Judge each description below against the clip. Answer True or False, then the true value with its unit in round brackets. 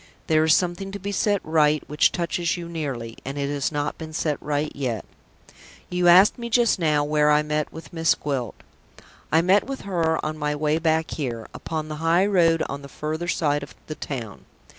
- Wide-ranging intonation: False (2.8 semitones)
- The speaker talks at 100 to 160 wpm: False (205 wpm)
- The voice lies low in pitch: False (155 Hz)